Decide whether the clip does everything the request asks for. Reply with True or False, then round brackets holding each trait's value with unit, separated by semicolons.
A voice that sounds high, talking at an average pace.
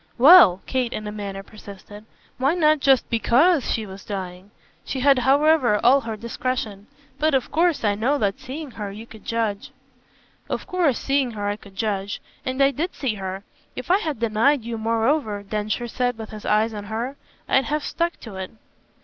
True (230 Hz; 190 wpm)